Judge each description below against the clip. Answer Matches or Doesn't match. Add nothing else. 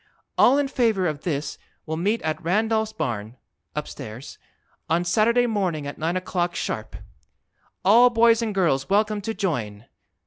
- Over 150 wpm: Doesn't match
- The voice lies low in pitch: Doesn't match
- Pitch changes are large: Matches